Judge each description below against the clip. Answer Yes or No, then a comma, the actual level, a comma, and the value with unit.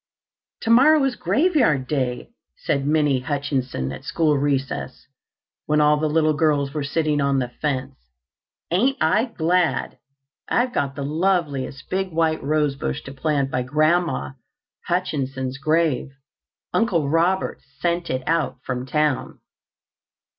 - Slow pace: Yes, slow, 125 wpm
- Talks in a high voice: No, medium, 150 Hz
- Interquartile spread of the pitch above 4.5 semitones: No, average, 3.7 semitones